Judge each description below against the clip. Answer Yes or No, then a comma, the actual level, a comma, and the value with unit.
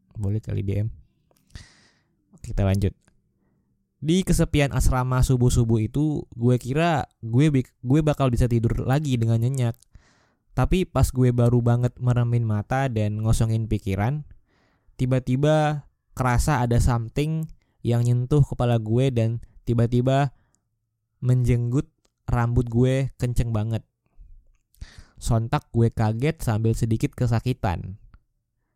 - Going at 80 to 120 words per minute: Yes, average, 105 wpm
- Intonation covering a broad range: No, narrow, 2.4 semitones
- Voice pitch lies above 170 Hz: No, low, 120 Hz